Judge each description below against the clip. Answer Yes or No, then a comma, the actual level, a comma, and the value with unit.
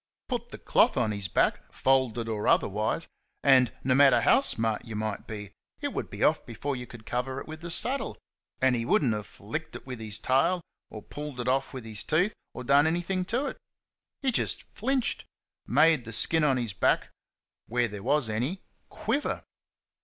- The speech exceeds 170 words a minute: Yes, average, 195 wpm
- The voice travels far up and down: Yes, wide, 6.0 semitones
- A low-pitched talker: Yes, low, 130 Hz